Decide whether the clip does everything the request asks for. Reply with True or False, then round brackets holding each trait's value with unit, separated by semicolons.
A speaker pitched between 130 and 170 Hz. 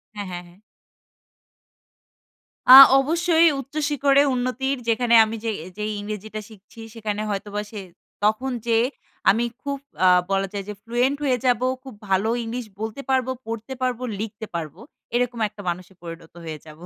False (225 Hz)